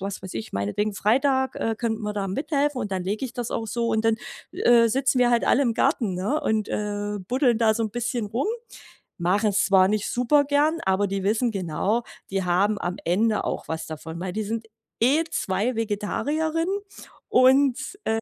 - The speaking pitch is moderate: No, high, 220 Hz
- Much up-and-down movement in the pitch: No, average, 4.2 semitones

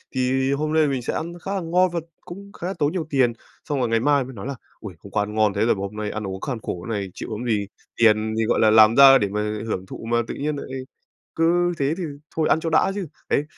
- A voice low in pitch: Yes, low, 130 Hz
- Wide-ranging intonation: Yes, wide, 6.5 semitones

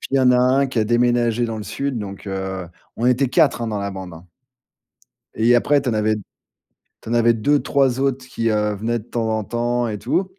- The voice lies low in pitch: Yes, low, 120 Hz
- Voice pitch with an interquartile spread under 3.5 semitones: Yes, average, 2.9 semitones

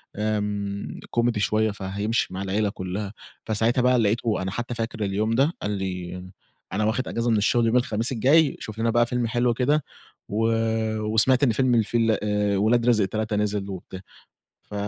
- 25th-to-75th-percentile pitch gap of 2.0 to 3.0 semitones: Yes, narrow, 2.6 semitones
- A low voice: Yes, low, 110 Hz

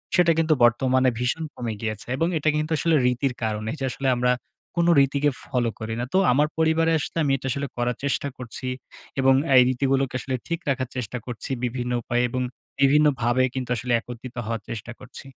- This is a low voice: Yes, low, 130 Hz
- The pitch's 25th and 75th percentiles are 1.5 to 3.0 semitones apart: Yes, average, 2.7 semitones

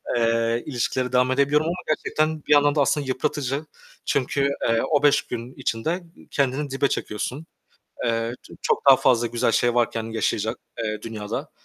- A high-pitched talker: No, low, 130 Hz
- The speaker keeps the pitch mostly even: No, average, 4.0 semitones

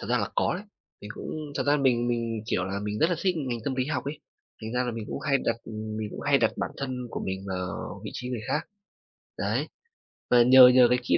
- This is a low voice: Yes, low, 125 Hz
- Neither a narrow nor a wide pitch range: Yes, average, 3.8 semitones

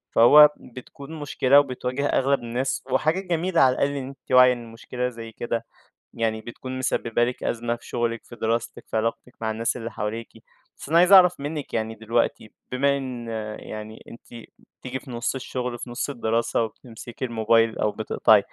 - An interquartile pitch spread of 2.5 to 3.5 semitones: Yes, average, 3.0 semitones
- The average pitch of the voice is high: No, low, 125 Hz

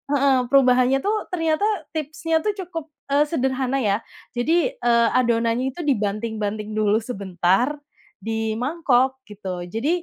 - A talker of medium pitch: No, very high, 255 Hz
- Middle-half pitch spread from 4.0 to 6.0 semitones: Yes, average, 5.2 semitones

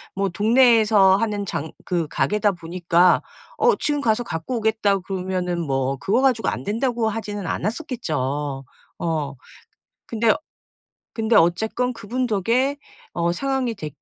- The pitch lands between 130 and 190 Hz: No, high, 205 Hz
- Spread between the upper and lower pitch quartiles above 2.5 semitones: Yes, average, 5.1 semitones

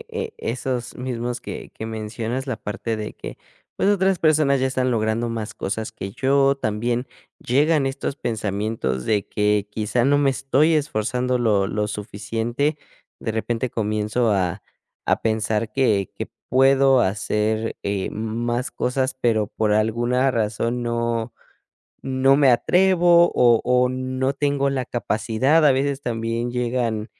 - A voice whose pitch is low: Yes, low, 120 Hz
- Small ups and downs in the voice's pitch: No, average, 3.5 semitones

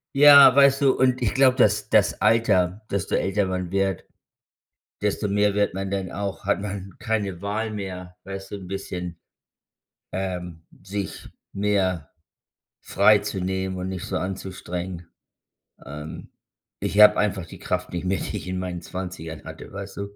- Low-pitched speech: Yes, very low, 95 Hz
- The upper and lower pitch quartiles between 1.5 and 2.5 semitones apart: Yes, narrow, 2.1 semitones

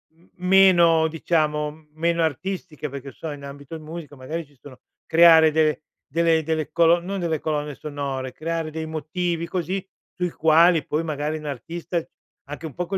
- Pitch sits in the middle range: Yes, medium, 160 Hz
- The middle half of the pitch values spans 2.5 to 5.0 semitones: No, narrow, 2.1 semitones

